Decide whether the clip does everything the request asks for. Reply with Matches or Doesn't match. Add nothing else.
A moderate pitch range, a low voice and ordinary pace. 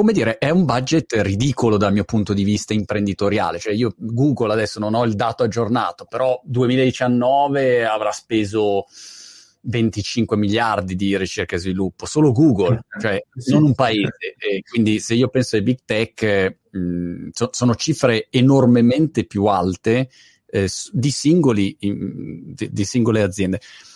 Matches